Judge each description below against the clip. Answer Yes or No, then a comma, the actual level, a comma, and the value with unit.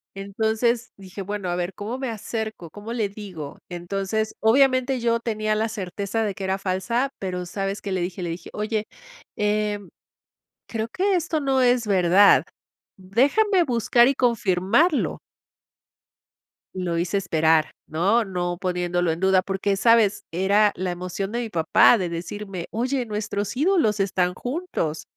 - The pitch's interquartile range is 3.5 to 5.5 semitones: Yes, average, 4.0 semitones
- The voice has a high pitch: Yes, high, 205 Hz